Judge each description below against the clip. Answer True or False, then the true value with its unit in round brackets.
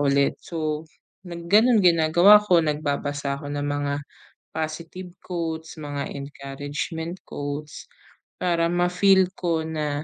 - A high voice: False (160 Hz)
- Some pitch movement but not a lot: True (3.3 semitones)